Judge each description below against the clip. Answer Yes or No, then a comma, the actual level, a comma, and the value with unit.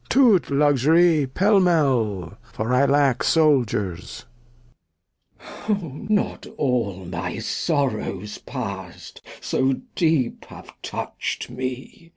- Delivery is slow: Yes, slow, 95 wpm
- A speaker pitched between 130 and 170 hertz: Yes, low, 135 Hz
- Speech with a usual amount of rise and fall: No, wide, 6.4 semitones